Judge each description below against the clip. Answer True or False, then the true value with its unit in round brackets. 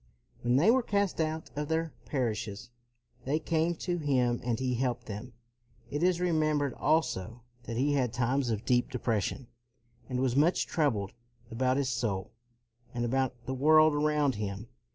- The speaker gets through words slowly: False (160 wpm)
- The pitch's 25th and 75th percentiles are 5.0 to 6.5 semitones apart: False (4.4 semitones)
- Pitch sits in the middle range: False (130 Hz)